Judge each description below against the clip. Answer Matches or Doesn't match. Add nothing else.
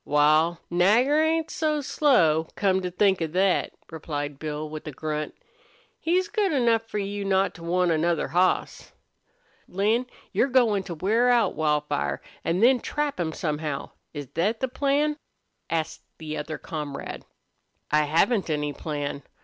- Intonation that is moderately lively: Doesn't match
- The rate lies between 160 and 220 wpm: Doesn't match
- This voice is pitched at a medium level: Matches